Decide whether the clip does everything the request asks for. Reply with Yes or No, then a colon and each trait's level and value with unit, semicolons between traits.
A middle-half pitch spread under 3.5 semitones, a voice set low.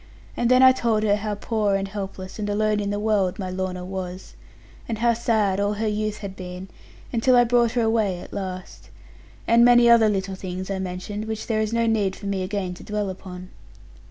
No: average, 2.8 semitones; high, 205 Hz